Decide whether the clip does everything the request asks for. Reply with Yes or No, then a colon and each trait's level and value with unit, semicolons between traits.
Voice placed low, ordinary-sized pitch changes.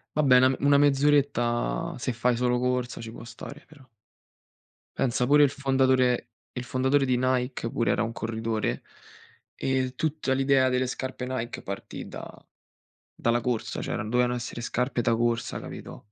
No: low, 125 Hz; narrow, 2.1 semitones